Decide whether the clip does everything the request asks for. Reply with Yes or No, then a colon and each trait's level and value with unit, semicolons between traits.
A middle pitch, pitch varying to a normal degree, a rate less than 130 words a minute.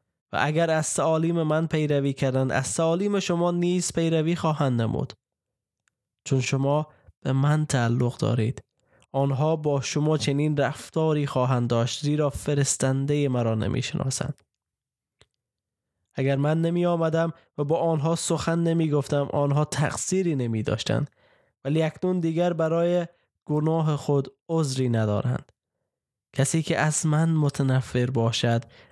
Yes: medium, 145 Hz; average, 3.6 semitones; average, 120 wpm